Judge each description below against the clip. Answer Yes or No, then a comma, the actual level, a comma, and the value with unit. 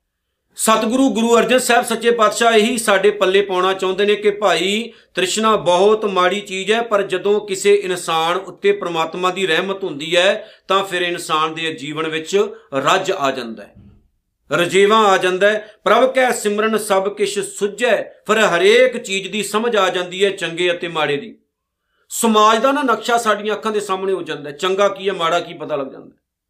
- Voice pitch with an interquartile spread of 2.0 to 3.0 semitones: No, average, 3.4 semitones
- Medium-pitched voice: No, high, 195 Hz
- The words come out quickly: Yes, fast, 180 wpm